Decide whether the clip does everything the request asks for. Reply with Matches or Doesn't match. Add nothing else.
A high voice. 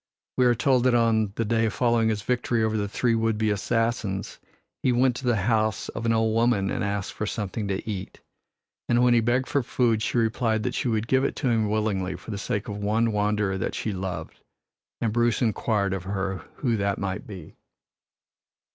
Doesn't match